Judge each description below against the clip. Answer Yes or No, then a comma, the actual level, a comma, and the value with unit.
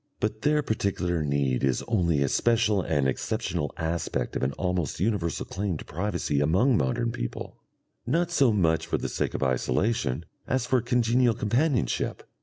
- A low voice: Yes, very low, 95 Hz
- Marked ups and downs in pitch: Yes, wide, 8.0 semitones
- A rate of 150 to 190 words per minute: Yes, average, 160 wpm